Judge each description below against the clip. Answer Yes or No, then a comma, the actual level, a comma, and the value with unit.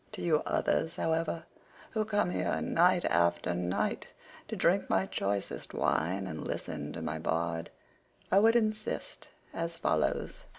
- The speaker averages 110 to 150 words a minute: Yes, average, 140 wpm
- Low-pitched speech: Yes, low, 100 Hz